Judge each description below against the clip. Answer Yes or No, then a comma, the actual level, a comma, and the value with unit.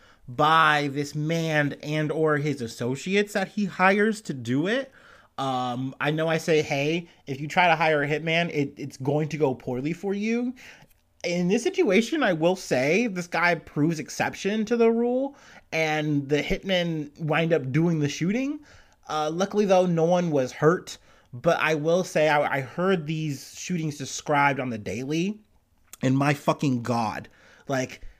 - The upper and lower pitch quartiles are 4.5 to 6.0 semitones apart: No, average, 4.0 semitones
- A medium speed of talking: Yes, average, 170 wpm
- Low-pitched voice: No, medium, 155 Hz